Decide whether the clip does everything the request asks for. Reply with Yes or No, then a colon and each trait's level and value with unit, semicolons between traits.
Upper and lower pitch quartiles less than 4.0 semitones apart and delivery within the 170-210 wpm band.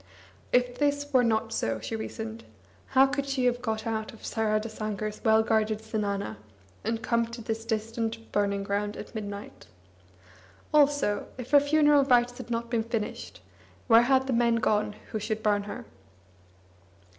No: narrow, 2.5 semitones; average, 155 wpm